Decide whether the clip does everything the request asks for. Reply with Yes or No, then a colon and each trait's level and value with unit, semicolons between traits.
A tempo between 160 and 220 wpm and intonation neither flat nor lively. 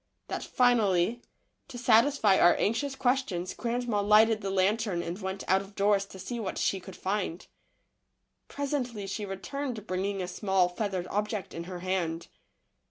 Yes: average, 170 wpm; average, 3.6 semitones